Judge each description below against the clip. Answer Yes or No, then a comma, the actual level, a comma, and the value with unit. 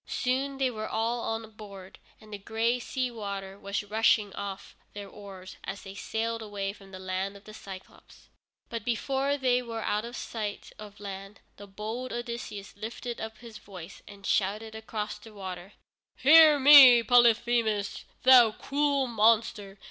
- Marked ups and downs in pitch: No, average, 3.0 semitones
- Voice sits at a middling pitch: No, high, 220 Hz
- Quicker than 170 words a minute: No, average, 160 wpm